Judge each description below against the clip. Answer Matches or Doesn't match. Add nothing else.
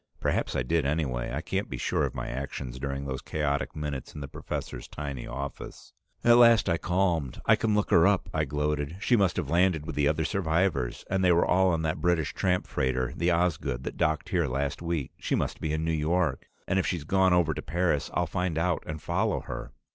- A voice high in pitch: Doesn't match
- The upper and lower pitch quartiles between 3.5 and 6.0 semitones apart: Matches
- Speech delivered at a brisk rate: Matches